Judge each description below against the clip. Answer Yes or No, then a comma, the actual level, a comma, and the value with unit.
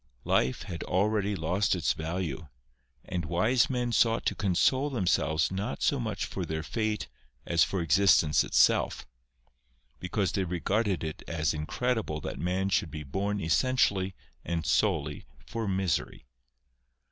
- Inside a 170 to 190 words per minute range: No, slow, 135 wpm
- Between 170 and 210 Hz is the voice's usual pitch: No, very low, 95 Hz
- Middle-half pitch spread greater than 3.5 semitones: Yes, average, 4.5 semitones